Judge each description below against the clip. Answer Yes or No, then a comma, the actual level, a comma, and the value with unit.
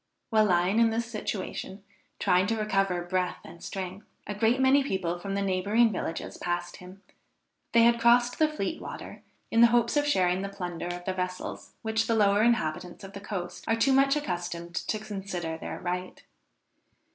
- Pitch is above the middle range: Yes, high, 200 Hz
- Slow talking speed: No, average, 180 wpm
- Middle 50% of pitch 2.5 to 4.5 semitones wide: Yes, average, 4.1 semitones